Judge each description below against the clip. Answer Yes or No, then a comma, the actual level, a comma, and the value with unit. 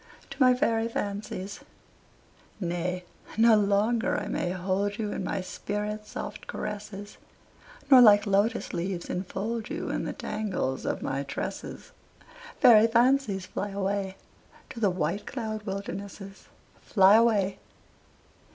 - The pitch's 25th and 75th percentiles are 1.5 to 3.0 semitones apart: Yes, narrow, 2.4 semitones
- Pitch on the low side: No, high, 205 Hz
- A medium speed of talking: No, slow, 125 wpm